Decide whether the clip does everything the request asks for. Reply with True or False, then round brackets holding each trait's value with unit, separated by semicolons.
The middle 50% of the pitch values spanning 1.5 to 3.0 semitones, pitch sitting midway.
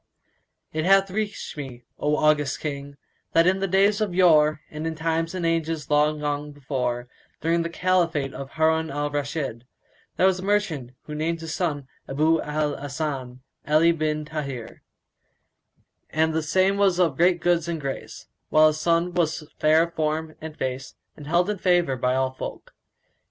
True (2.6 semitones; 155 Hz)